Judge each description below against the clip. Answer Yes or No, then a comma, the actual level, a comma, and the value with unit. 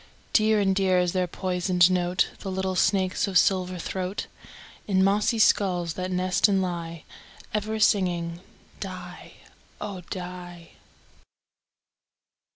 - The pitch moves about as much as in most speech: No, narrow, 1.6 semitones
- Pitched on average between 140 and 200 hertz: Yes, medium, 185 Hz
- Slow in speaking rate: Yes, slow, 120 wpm